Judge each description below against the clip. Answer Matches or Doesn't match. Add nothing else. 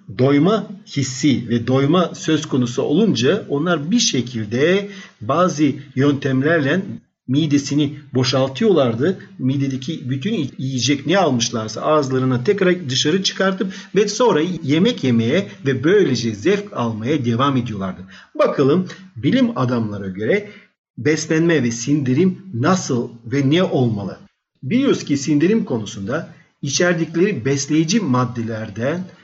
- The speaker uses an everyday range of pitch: Doesn't match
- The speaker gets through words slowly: Doesn't match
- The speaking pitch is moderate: Matches